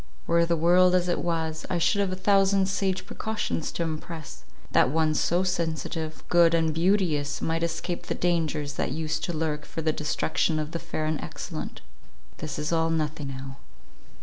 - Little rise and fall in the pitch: Yes, narrow, 2.3 semitones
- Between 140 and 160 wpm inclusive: No, average, 180 wpm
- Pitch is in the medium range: Yes, medium, 165 Hz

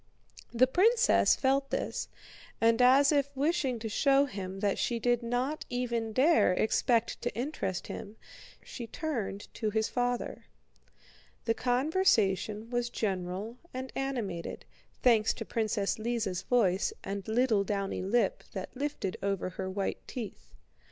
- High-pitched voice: Yes, high, 235 Hz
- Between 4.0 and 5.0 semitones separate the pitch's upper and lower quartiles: Yes, average, 4.4 semitones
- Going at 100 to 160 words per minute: Yes, slow, 135 wpm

